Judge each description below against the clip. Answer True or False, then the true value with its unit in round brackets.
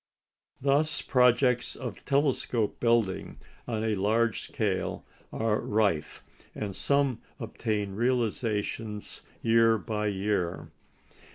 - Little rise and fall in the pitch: False (3.0 semitones)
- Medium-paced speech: False (95 wpm)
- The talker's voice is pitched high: False (110 Hz)